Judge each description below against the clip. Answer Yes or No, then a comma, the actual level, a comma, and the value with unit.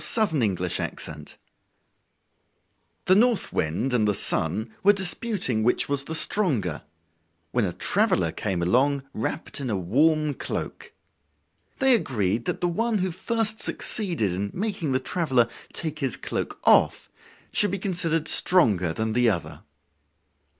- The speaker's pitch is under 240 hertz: Yes, medium, 140 Hz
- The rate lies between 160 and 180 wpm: No, slow, 135 wpm